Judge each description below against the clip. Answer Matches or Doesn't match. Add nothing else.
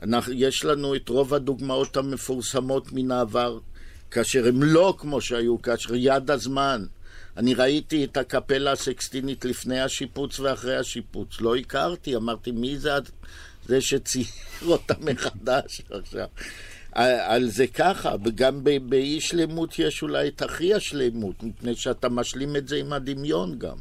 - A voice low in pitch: Matches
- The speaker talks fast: Doesn't match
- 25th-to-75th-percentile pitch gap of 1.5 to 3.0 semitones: Matches